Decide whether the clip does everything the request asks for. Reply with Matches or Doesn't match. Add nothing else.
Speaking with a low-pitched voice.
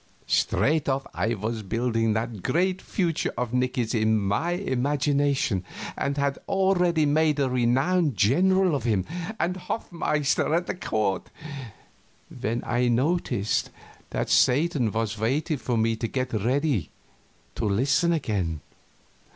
Matches